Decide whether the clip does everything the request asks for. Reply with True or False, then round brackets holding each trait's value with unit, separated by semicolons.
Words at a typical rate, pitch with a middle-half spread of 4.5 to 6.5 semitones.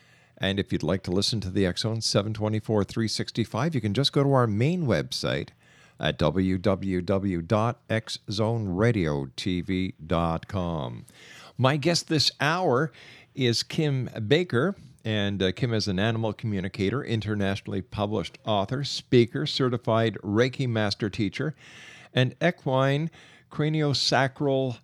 False (110 wpm; 5.2 semitones)